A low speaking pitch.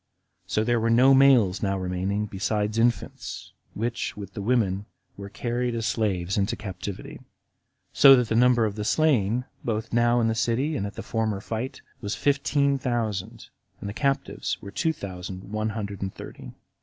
Yes: low, 110 Hz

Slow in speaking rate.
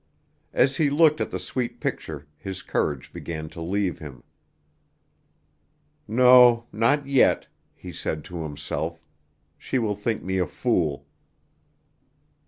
Yes: slow, 125 wpm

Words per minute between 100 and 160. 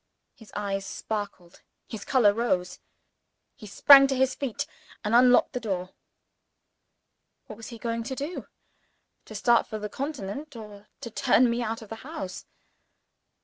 Yes: average, 150 wpm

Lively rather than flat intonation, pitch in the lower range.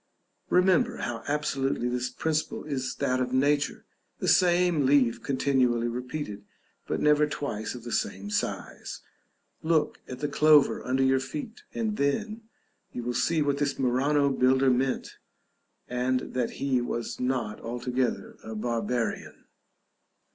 No: average, 3.1 semitones; low, 130 Hz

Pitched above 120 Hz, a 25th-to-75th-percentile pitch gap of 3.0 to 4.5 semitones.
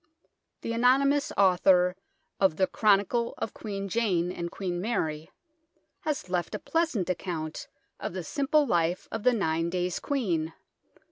No: high, 190 Hz; average, 5.3 semitones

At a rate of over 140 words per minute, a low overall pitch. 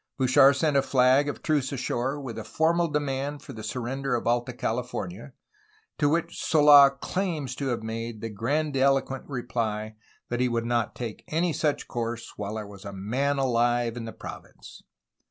Yes: average, 175 wpm; low, 130 Hz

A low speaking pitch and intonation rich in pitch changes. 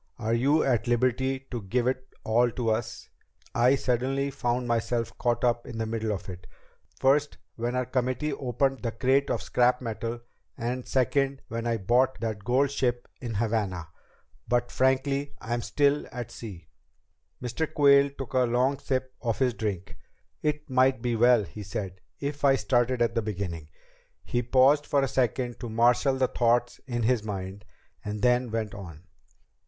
No: low, 120 Hz; narrow, 2.6 semitones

